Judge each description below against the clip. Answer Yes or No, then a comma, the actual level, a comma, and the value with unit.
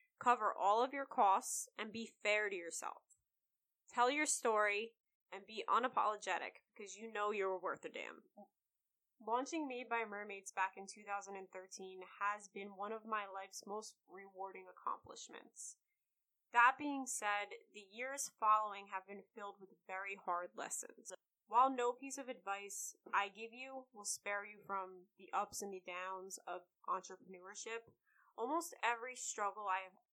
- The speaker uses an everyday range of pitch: Yes, average, 3.7 semitones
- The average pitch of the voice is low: No, high, 205 Hz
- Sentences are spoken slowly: No, average, 150 wpm